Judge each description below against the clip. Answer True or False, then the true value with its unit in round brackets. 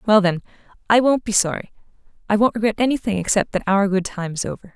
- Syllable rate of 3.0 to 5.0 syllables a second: False (6.5 syllables/s)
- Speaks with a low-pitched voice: False (205 Hz)